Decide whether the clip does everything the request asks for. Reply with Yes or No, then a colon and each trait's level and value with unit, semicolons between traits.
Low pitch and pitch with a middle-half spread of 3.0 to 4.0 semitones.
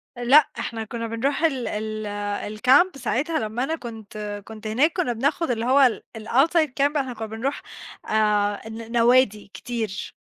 No: high, 235 Hz; average, 3.7 semitones